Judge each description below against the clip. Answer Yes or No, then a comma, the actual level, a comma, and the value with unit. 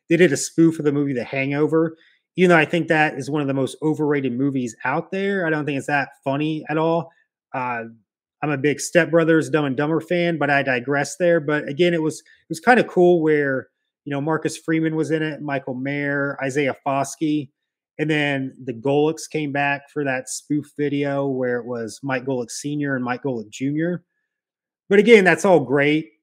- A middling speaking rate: No, fast, 210 wpm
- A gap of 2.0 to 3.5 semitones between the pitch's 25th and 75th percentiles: Yes, average, 2.7 semitones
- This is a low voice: No, medium, 145 Hz